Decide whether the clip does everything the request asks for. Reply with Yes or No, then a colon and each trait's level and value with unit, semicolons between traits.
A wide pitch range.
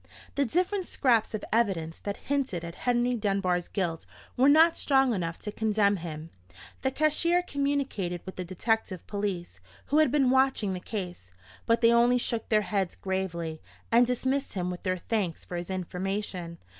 Yes: wide, 6.0 semitones